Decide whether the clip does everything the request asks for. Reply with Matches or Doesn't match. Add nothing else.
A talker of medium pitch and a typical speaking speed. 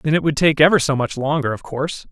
Doesn't match